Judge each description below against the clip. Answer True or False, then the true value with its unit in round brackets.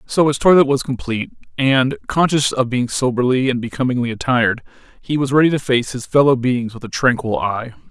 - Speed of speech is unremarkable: True (190 wpm)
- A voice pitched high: False (130 Hz)